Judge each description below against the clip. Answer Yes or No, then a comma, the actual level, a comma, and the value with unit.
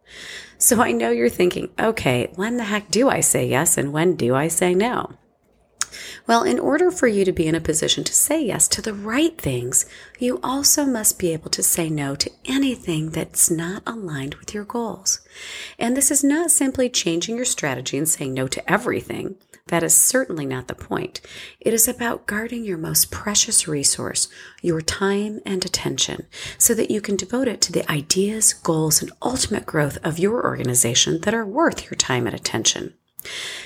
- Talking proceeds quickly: No, average, 190 wpm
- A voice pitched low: No, medium, 185 Hz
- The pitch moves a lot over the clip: Yes, wide, 6.8 semitones